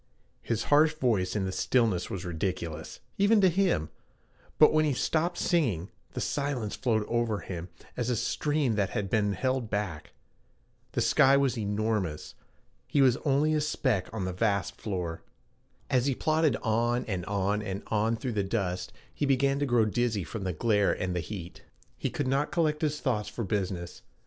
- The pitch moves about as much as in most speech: No, wide, 6.0 semitones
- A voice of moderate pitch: No, low, 110 Hz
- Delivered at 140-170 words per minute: No, average, 180 wpm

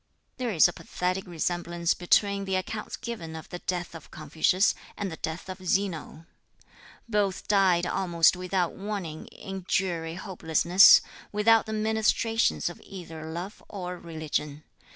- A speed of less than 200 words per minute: Yes, average, 140 wpm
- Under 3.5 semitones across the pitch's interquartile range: Yes, average, 3.1 semitones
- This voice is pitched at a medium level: Yes, medium, 180 Hz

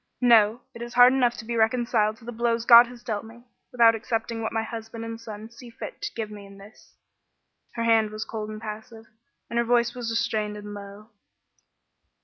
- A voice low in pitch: No, high, 225 Hz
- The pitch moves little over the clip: Yes, narrow, 1.6 semitones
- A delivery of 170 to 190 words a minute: No, fast, 205 wpm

